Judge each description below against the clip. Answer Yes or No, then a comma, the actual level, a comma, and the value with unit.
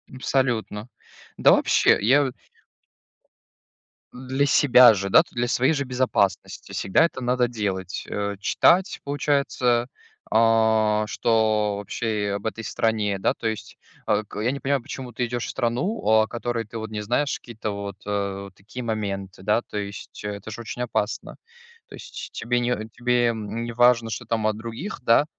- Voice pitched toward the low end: Yes, low, 115 Hz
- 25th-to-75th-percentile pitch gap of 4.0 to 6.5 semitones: No, average, 2.9 semitones